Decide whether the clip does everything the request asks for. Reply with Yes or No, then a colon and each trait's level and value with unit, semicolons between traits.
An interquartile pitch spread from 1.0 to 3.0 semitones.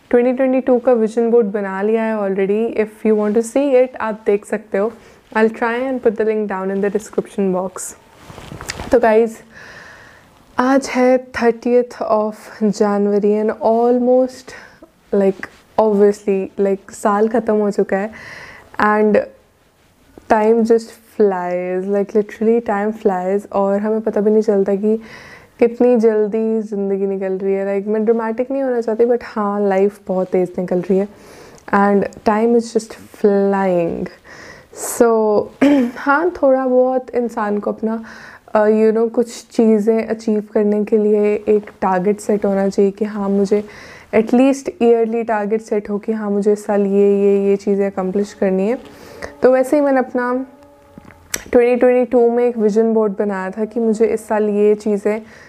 Yes: narrow, 2.5 semitones